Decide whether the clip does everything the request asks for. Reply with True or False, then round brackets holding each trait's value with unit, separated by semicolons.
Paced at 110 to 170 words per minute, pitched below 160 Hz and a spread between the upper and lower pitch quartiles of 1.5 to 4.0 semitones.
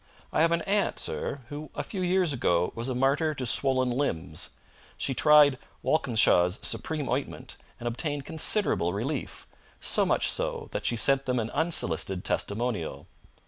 False (155 wpm; 135 Hz; 4.9 semitones)